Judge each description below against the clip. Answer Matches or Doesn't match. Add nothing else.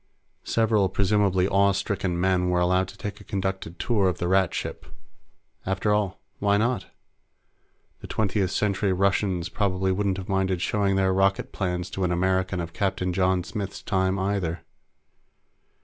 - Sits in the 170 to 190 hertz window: Doesn't match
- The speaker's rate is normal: Matches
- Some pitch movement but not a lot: Doesn't match